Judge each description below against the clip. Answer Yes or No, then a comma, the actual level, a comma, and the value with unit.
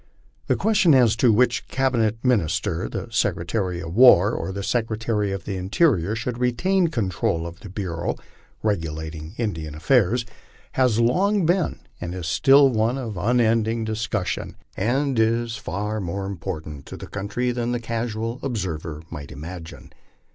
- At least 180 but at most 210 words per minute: No, average, 155 wpm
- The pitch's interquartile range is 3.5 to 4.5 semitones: No, average, 5.2 semitones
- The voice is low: Yes, low, 110 Hz